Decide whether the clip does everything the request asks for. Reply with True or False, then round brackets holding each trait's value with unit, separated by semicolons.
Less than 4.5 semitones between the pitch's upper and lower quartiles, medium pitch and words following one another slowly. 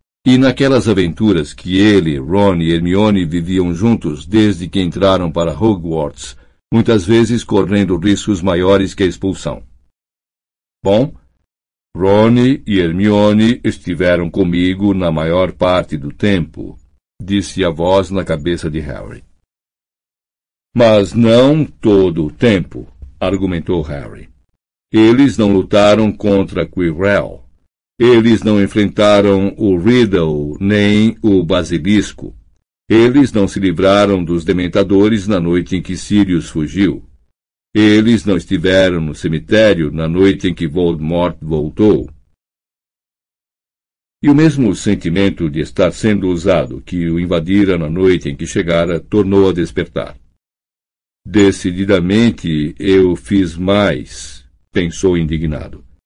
False (3.7 semitones; 95 Hz; 115 wpm)